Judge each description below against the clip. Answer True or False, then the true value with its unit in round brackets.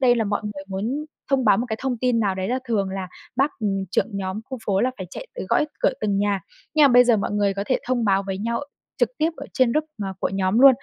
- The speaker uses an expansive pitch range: False (4.3 semitones)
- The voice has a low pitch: False (215 Hz)